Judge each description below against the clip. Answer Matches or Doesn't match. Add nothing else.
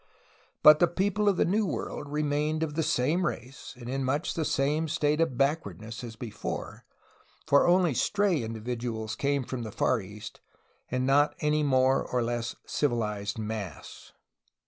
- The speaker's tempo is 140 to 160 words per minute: Doesn't match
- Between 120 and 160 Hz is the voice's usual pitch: Matches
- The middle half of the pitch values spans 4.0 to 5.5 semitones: Matches